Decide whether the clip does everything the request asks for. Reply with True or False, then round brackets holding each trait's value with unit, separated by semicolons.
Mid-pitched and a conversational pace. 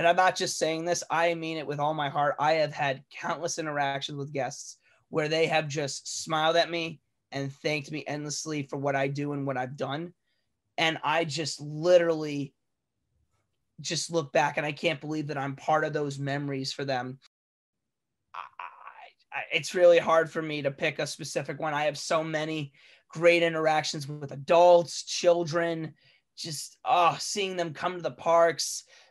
True (155 Hz; 180 wpm)